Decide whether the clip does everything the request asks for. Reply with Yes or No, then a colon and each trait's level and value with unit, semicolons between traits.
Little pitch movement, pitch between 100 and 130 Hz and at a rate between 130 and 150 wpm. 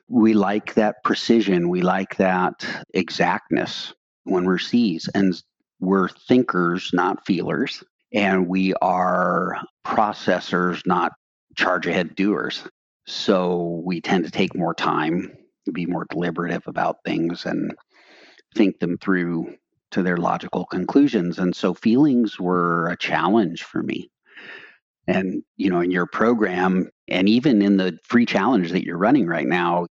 No: narrow, 2.3 semitones; very low, 90 Hz; average, 140 wpm